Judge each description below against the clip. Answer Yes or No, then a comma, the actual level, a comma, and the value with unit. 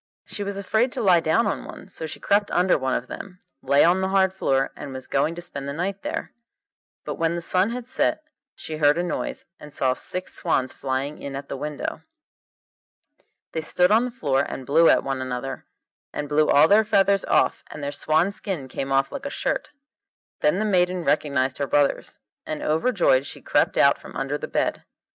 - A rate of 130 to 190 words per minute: No, fast, 205 wpm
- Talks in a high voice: No, medium, 160 Hz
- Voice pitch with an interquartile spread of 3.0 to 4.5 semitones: No, wide, 5.4 semitones